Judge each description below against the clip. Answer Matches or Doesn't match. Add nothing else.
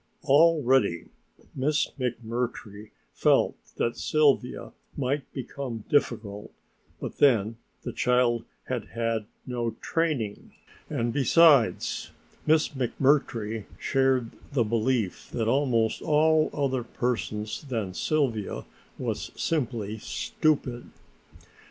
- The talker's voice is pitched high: Doesn't match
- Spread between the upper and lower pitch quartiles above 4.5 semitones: Doesn't match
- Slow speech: Matches